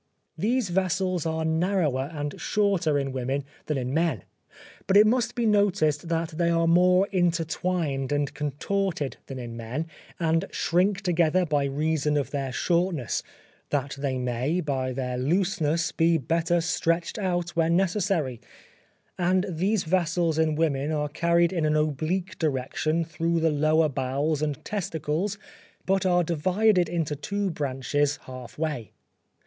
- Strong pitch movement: No, average, 3.7 semitones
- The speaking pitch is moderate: Yes, medium, 160 Hz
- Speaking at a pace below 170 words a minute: Yes, average, 145 wpm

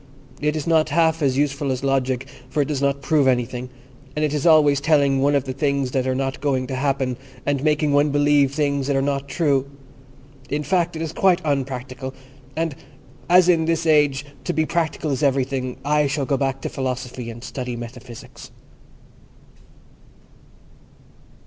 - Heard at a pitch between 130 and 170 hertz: Yes, medium, 140 Hz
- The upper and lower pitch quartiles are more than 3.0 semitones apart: No, narrow, 2.4 semitones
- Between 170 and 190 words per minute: Yes, average, 175 wpm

